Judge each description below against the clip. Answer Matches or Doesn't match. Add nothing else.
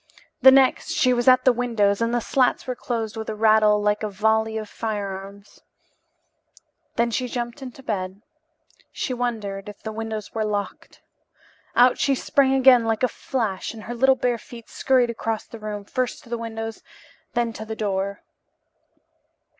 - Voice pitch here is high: Matches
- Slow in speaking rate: Doesn't match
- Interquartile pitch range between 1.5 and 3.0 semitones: Matches